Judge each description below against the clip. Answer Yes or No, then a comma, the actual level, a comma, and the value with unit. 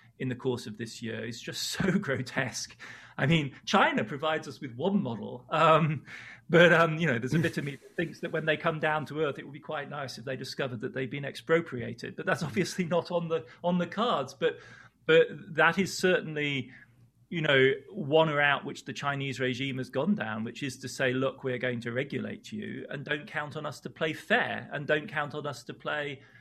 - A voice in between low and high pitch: Yes, medium, 145 Hz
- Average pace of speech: No, fast, 225 wpm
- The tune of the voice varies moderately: Yes, average, 4.2 semitones